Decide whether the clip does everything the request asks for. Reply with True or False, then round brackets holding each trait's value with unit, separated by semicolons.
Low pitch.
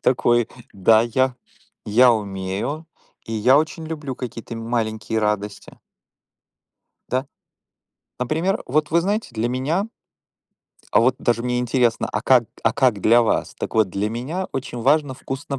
True (120 Hz)